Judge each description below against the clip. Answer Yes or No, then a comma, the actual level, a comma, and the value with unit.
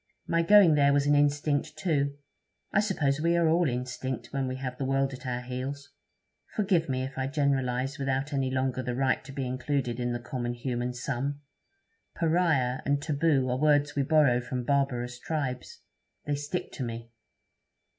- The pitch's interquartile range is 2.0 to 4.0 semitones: Yes, narrow, 2.5 semitones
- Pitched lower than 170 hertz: Yes, low, 135 Hz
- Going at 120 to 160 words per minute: No, average, 175 wpm